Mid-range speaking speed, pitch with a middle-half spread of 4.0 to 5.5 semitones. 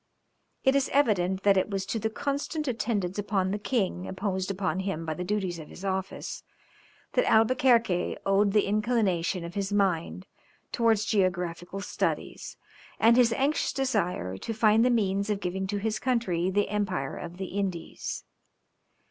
No: average, 160 wpm; average, 3.2 semitones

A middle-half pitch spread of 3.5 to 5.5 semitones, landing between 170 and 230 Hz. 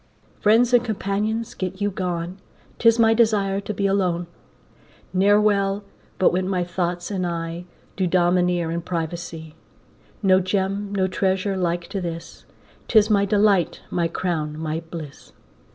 No: average, 2.8 semitones; medium, 185 Hz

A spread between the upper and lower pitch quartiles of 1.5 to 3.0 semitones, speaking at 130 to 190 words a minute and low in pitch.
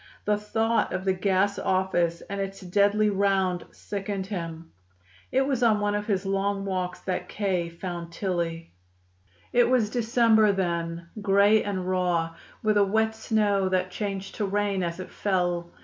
No: narrow, 2.4 semitones; average, 160 wpm; high, 195 Hz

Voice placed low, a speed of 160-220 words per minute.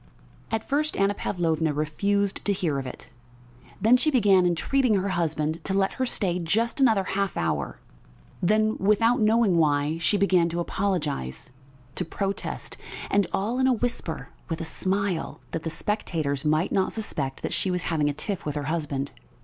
No: medium, 185 Hz; average, 175 wpm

